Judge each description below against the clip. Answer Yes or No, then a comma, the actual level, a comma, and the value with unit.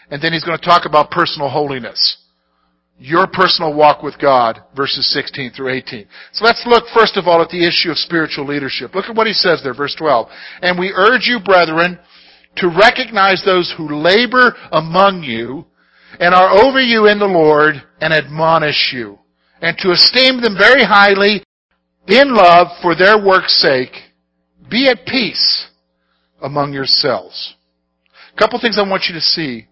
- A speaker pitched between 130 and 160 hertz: No, medium, 170 Hz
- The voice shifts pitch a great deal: Yes, wide, 6.4 semitones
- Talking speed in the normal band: Yes, average, 175 wpm